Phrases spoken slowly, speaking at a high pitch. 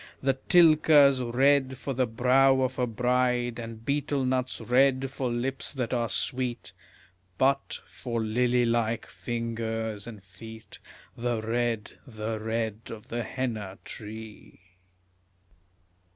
No: slow, 125 wpm; low, 120 Hz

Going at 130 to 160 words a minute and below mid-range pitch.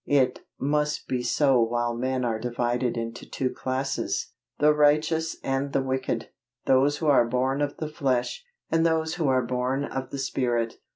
No: average, 170 wpm; low, 130 Hz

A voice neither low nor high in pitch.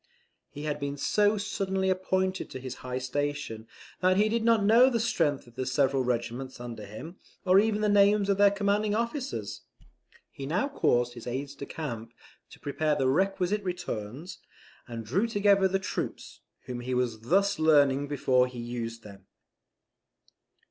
Yes: medium, 150 Hz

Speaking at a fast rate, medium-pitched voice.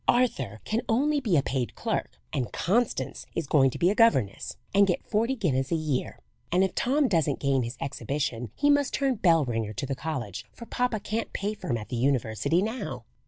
Yes: fast, 210 wpm; medium, 165 Hz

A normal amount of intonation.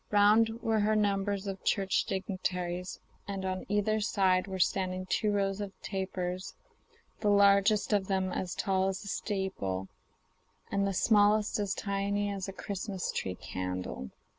No: narrow, 1.7 semitones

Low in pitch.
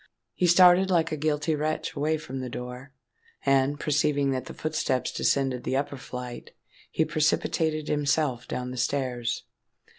No: medium, 145 Hz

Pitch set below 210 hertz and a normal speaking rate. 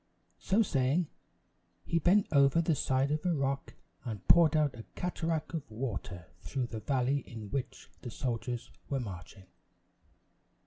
Yes: low, 135 Hz; average, 145 wpm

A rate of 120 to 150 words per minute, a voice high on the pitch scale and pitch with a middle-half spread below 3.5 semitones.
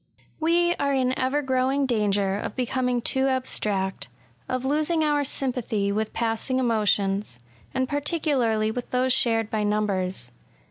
No: average, 145 wpm; very high, 250 Hz; average, 4.3 semitones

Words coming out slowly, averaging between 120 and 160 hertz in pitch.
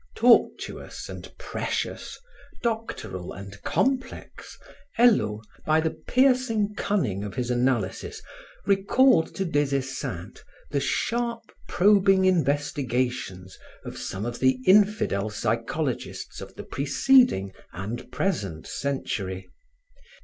Yes: slow, 100 wpm; medium, 140 Hz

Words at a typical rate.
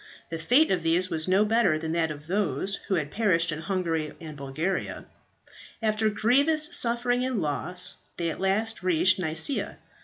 Yes: average, 165 wpm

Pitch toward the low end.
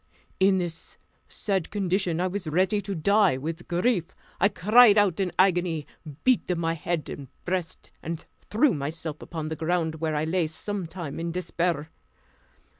No: medium, 175 Hz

